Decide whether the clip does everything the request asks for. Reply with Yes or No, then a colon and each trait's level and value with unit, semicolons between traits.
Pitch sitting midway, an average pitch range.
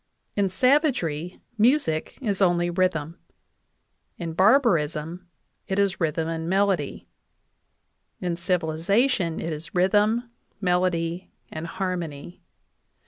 Yes: medium, 180 Hz; average, 3.4 semitones